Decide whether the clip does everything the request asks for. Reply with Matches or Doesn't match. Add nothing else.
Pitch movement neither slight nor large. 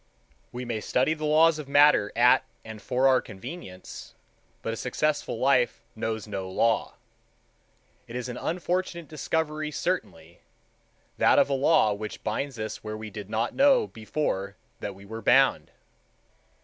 Doesn't match